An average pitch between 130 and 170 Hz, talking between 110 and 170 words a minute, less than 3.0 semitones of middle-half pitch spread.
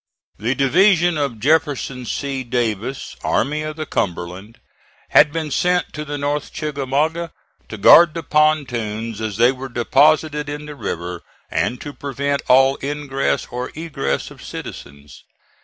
No: medium, 140 Hz; average, 140 wpm; average, 4.3 semitones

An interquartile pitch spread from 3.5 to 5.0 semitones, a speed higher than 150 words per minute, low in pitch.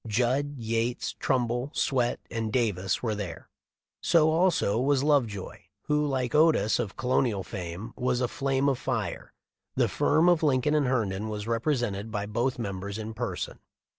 Yes: average, 4.3 semitones; average, 165 wpm; low, 120 Hz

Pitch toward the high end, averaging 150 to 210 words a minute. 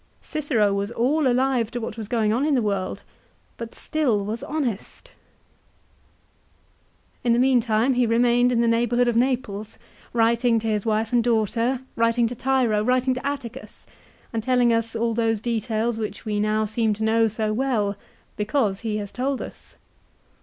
Yes: high, 230 Hz; average, 170 wpm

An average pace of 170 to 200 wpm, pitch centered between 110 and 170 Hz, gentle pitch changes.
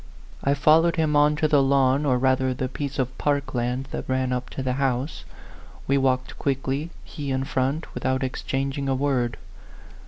Yes: average, 185 wpm; low, 135 Hz; narrow, 1.7 semitones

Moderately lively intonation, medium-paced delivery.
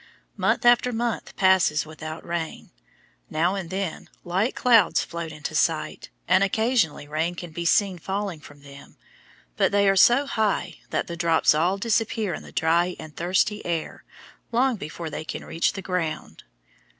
Yes: average, 4.2 semitones; average, 160 wpm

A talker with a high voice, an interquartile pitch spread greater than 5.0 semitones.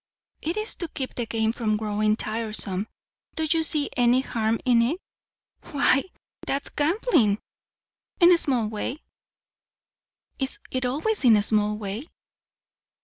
Yes: high, 245 Hz; wide, 5.6 semitones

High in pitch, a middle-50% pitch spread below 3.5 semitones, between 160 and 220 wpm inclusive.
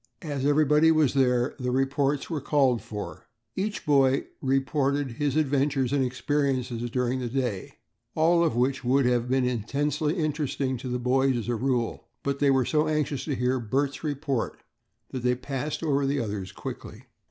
No: low, 135 Hz; narrow, 2.6 semitones; average, 170 wpm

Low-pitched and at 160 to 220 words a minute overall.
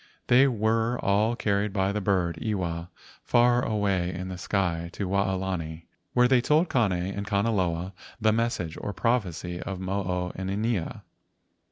No: low, 100 Hz; average, 150 wpm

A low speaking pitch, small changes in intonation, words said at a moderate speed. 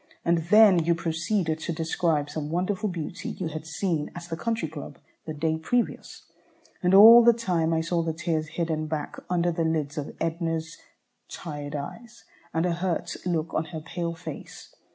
No: medium, 165 Hz; narrow, 2.1 semitones; average, 175 wpm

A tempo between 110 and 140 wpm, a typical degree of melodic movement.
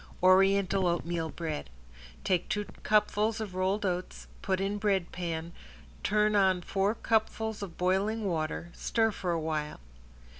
Yes: slow, 135 wpm; average, 3.2 semitones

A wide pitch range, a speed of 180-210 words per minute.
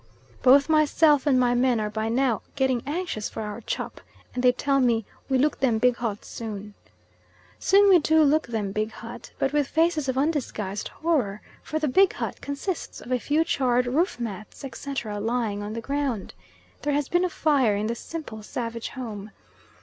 No: average, 4.9 semitones; average, 190 wpm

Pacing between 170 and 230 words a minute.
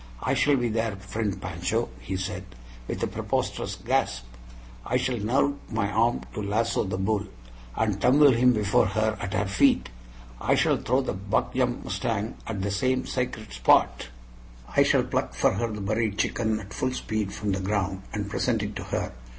Yes: average, 185 wpm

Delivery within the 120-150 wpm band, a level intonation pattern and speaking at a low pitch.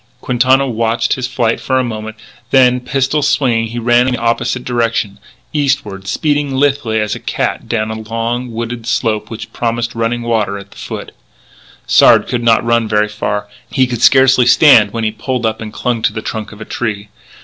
No: average, 195 wpm; narrow, 2.3 semitones; low, 115 Hz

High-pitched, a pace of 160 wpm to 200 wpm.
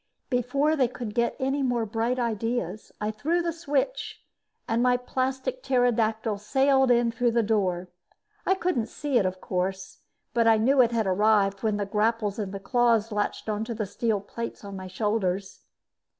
Yes: high, 230 Hz; average, 175 wpm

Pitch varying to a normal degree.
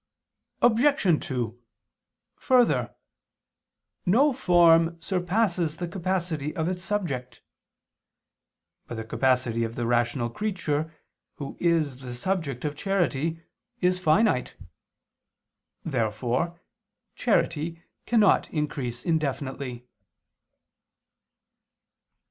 No: wide, 6.1 semitones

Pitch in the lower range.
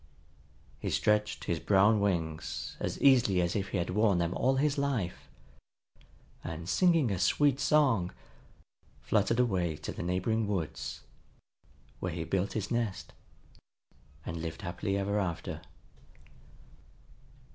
Yes: low, 100 Hz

